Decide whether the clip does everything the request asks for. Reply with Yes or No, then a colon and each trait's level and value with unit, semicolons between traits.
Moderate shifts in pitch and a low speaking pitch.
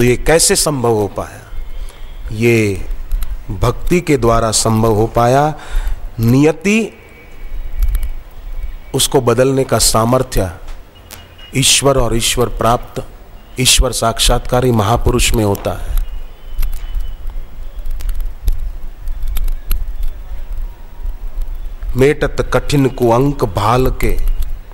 No: wide, 7.5 semitones; low, 110 Hz